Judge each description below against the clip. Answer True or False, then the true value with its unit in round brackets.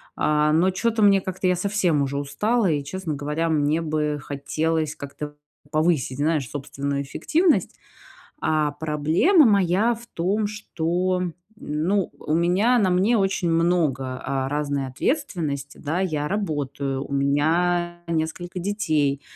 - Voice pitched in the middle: True (160 Hz)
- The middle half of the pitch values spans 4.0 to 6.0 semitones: True (4.4 semitones)